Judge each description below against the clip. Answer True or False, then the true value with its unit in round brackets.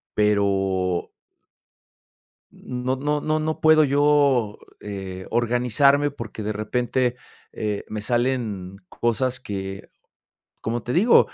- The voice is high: False (120 Hz)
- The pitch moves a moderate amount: True (5.0 semitones)